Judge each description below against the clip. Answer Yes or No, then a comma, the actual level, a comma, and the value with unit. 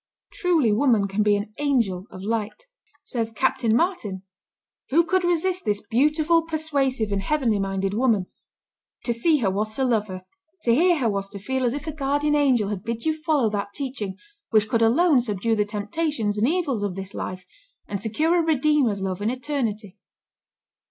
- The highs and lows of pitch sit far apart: Yes, wide, 6.4 semitones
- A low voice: No, high, 230 Hz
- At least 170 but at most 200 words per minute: Yes, average, 180 wpm